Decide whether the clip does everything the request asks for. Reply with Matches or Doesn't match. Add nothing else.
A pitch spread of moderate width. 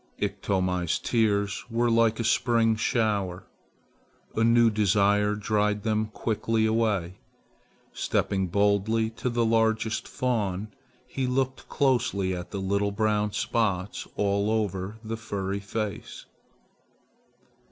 Doesn't match